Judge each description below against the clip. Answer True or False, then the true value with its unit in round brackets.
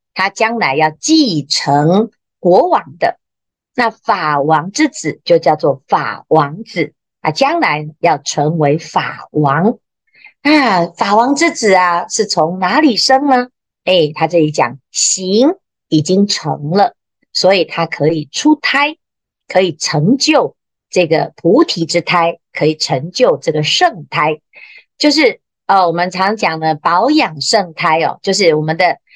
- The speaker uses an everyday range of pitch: False (7.9 semitones)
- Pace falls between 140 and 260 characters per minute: True (195 characters per minute)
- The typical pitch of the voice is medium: True (180 Hz)